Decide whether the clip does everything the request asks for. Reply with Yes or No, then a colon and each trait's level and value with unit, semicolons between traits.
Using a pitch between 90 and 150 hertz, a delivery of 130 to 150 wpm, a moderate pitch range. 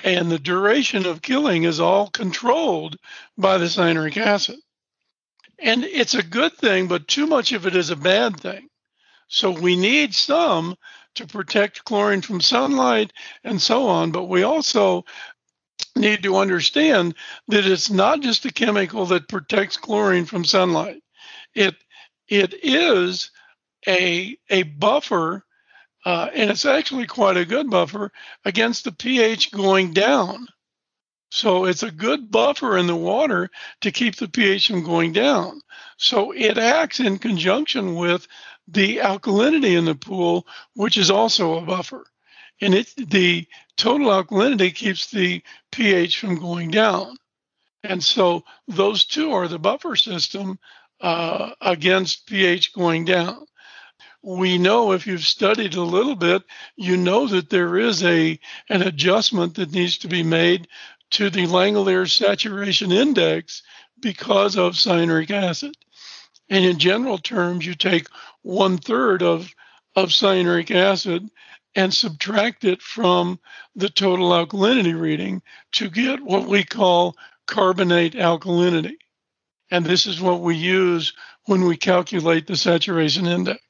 No: high, 195 Hz; average, 140 wpm; average, 4.0 semitones